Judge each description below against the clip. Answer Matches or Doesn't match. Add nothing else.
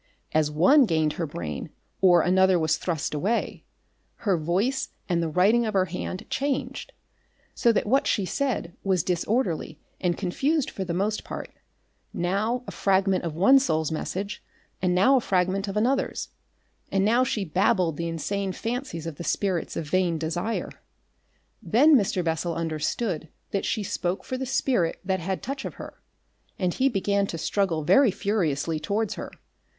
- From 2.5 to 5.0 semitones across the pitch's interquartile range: Matches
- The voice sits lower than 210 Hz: Matches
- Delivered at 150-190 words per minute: Matches